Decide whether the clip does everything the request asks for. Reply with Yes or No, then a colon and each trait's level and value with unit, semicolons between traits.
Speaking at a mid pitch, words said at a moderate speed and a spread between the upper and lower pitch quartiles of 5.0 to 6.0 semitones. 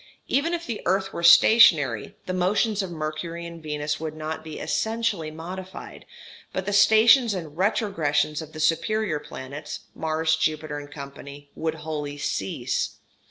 No: medium, 160 Hz; average, 145 wpm; average, 4.2 semitones